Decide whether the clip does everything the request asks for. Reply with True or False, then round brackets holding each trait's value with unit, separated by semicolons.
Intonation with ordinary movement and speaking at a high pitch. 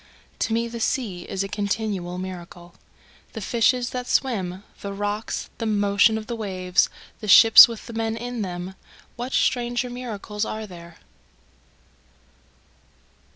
True (3.7 semitones; 215 Hz)